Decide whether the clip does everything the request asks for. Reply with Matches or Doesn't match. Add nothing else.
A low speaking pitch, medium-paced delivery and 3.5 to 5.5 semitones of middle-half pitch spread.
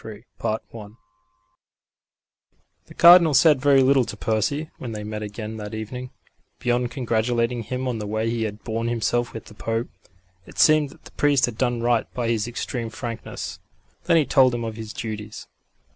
Doesn't match